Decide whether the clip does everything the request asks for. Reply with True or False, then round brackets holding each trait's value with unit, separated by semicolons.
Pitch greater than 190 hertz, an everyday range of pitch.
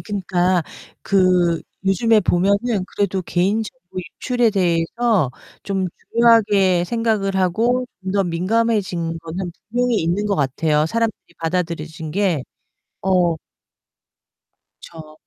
False (185 Hz; 4.0 semitones)